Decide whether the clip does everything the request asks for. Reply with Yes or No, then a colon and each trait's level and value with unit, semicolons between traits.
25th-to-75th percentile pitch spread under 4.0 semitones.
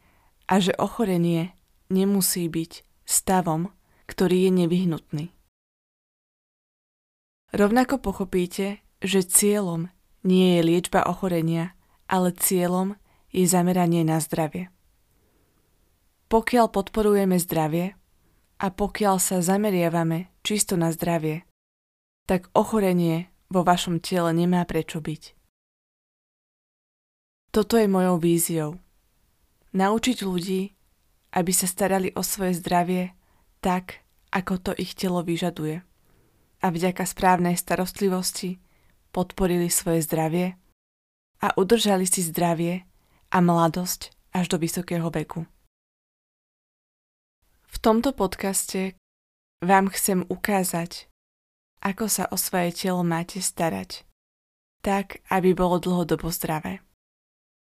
Yes: narrow, 2.4 semitones